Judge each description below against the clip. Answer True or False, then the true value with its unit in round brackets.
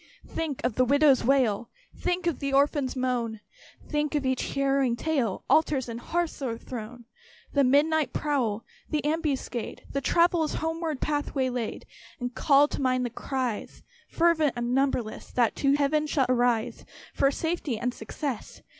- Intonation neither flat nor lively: True (3.5 semitones)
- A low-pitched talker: False (275 Hz)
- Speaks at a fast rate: False (150 wpm)